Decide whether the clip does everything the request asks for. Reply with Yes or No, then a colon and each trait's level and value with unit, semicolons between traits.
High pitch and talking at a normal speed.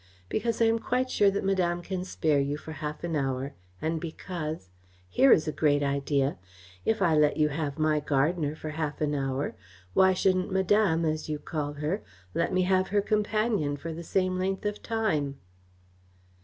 No: medium, 160 Hz; average, 185 wpm